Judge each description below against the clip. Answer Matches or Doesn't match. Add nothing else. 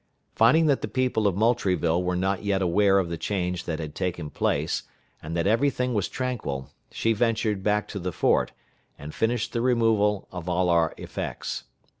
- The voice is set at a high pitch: Doesn't match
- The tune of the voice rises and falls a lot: Doesn't match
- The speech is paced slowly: Doesn't match